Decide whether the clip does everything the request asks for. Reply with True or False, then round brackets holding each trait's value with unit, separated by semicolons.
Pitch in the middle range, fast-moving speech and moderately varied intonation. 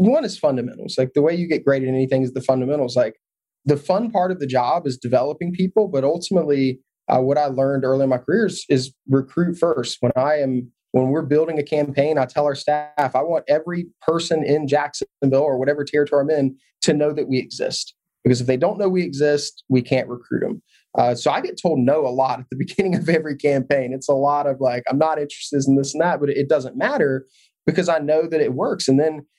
True (145 Hz; 235 wpm; 3.3 semitones)